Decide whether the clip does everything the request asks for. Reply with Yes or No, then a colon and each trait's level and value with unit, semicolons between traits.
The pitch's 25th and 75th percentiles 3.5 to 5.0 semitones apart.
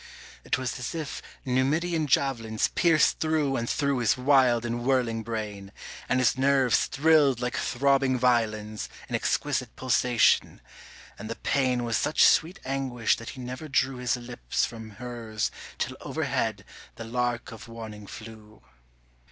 No: average, 2.9 semitones